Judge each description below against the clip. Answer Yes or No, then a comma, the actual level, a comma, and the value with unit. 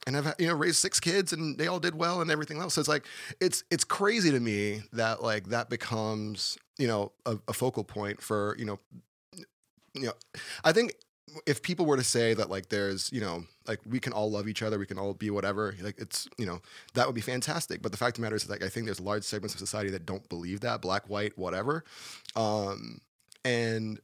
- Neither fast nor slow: No, fast, 240 wpm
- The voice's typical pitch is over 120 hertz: No, low, 110 Hz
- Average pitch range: No, wide, 6.0 semitones